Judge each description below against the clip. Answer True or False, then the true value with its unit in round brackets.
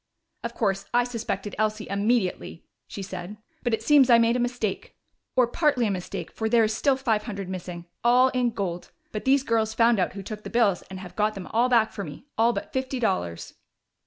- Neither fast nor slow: False (215 wpm)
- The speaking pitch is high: True (220 Hz)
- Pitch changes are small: False (3.7 semitones)